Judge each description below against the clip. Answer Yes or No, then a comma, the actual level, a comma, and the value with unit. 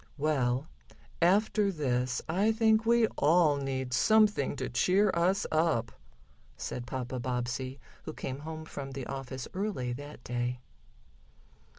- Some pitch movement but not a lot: No, wide, 6.5 semitones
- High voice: No, medium, 145 Hz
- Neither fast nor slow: No, slow, 125 wpm